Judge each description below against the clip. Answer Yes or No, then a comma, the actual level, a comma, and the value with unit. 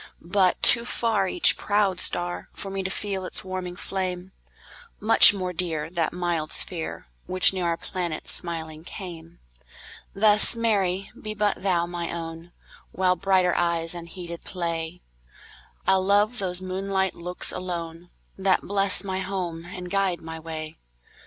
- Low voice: No, medium, 180 Hz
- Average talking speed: No, slow, 120 wpm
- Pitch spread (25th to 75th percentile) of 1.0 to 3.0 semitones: Yes, narrow, 2.4 semitones